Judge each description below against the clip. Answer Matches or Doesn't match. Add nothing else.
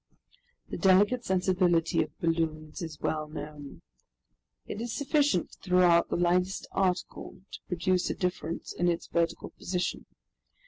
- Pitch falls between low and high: Matches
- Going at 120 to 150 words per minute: Matches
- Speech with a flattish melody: Matches